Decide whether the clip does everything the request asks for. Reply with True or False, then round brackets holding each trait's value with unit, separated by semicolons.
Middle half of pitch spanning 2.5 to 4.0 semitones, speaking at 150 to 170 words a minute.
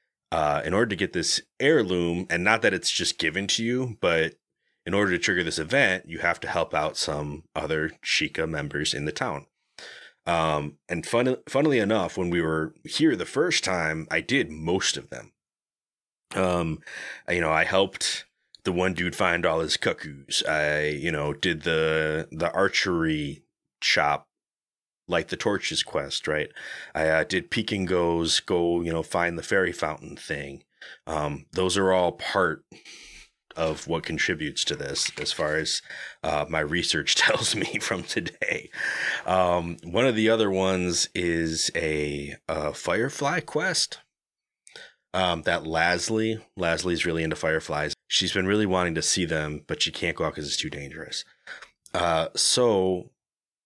True (2.8 semitones; 160 wpm)